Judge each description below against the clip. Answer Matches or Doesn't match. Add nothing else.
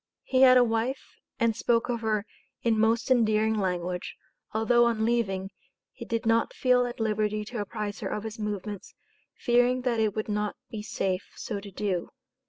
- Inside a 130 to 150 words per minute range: Doesn't match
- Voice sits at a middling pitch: Doesn't match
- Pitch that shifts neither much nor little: Doesn't match